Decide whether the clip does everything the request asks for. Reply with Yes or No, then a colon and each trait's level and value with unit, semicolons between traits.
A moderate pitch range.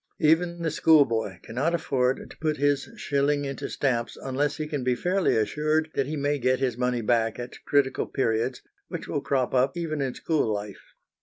Yes: average, 3.5 semitones